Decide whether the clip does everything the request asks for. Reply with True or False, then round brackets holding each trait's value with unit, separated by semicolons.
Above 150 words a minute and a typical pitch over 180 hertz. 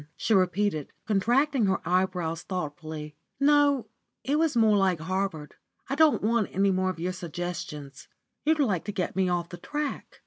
True (165 wpm; 190 Hz)